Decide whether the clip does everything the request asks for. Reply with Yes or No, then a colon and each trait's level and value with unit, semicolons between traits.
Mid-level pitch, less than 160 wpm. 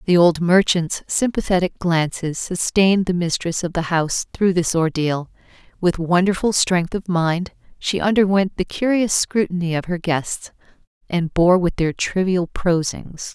Yes: medium, 175 Hz; average, 150 wpm